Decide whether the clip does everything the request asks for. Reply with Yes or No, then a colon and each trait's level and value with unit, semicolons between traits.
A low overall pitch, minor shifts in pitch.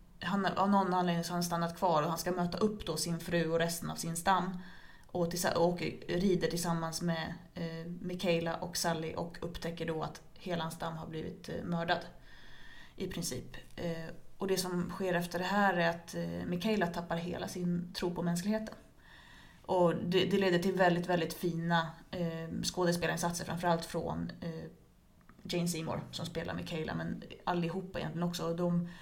No: medium, 175 Hz; narrow, 1.3 semitones